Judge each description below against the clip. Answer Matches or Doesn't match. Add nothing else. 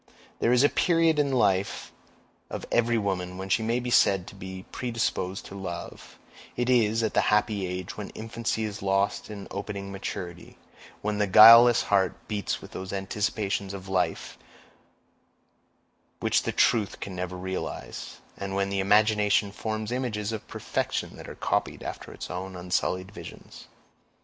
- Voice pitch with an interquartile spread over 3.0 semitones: Doesn't match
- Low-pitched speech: Matches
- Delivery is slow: Doesn't match